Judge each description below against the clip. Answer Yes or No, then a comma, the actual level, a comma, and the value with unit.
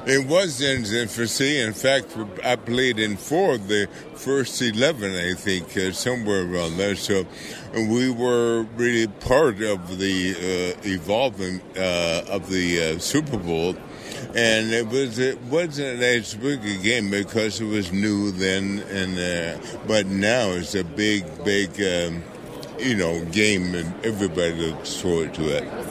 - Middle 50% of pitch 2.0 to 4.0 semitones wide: No, average, 4.4 semitones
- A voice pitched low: Yes, low, 105 Hz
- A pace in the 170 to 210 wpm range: No, average, 155 wpm